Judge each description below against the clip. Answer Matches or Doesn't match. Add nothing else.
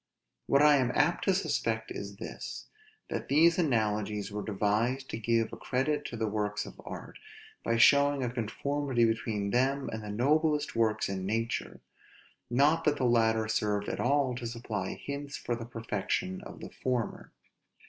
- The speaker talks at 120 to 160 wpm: Doesn't match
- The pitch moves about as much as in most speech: Matches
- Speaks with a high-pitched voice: Doesn't match